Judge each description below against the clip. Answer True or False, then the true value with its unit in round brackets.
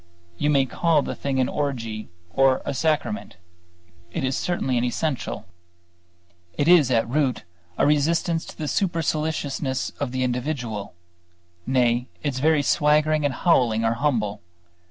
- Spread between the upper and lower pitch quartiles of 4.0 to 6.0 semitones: False (3.6 semitones)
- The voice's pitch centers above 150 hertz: False (140 Hz)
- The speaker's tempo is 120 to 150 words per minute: True (140 wpm)